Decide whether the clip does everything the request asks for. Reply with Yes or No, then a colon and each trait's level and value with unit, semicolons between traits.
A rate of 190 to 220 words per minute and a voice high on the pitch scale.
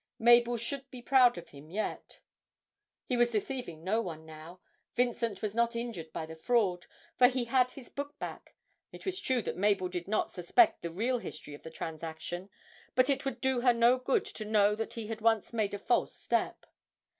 Yes: average, 200 wpm; high, 225 Hz